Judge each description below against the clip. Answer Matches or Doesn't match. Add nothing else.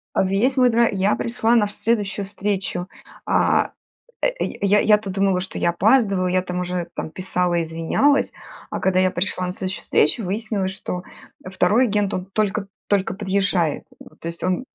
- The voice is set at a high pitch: Matches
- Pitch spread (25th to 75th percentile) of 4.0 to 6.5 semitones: Doesn't match